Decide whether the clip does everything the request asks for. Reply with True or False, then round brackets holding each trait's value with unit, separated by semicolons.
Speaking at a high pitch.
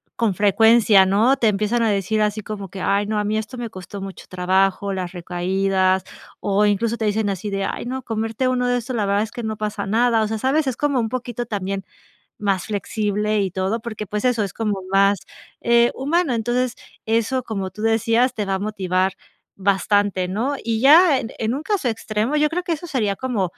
True (215 Hz)